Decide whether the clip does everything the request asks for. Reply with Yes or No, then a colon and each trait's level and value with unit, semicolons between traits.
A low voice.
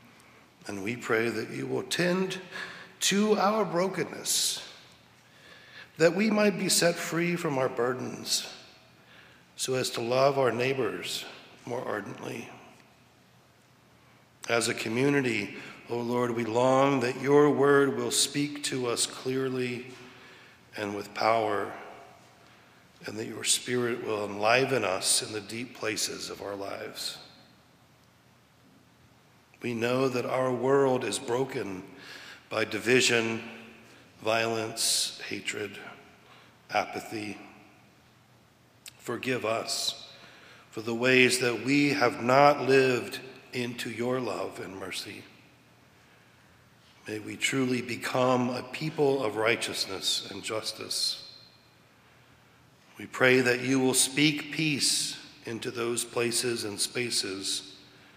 Yes: low, 125 Hz